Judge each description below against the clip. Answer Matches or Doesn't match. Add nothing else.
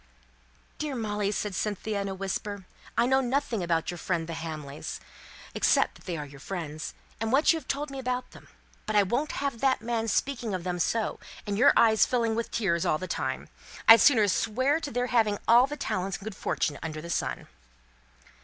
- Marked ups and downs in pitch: Matches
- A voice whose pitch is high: Matches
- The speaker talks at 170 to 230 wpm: Matches